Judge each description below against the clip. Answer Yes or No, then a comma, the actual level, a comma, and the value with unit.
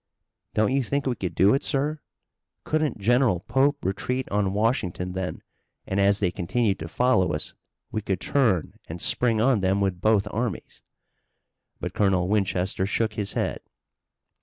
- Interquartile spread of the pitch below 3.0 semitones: No, average, 4.8 semitones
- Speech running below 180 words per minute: Yes, average, 160 wpm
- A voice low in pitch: Yes, low, 105 Hz